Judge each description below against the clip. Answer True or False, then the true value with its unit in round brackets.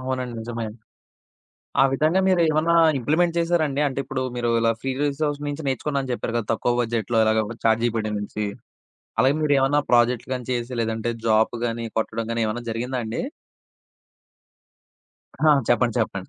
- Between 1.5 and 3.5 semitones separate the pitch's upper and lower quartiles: False (3.9 semitones)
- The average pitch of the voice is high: False (125 Hz)